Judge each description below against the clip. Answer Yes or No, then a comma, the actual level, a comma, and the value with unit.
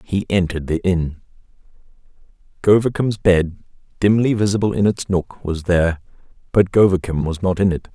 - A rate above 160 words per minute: No, average, 145 wpm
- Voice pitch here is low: Yes, very low, 95 Hz